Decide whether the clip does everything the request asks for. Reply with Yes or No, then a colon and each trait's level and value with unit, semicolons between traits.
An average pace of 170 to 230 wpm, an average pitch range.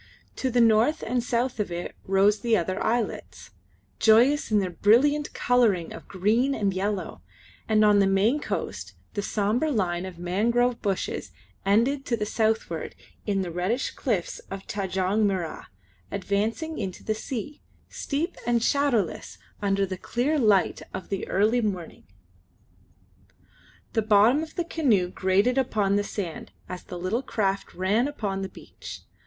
No: average, 150 wpm; average, 4.0 semitones